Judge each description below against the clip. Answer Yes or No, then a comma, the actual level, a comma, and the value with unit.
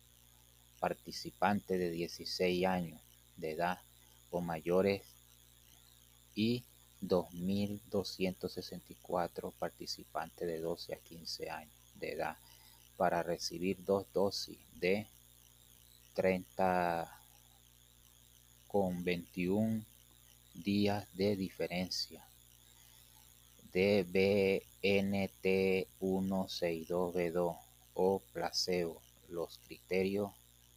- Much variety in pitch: Yes, wide, 7.9 semitones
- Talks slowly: Yes, slow, 70 wpm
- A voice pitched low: Yes, very low, 85 Hz